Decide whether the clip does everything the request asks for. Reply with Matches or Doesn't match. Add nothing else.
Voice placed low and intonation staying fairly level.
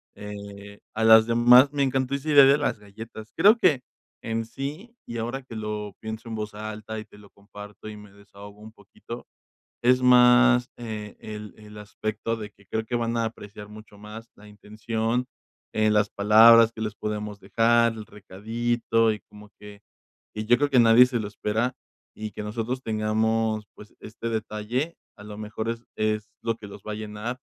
Matches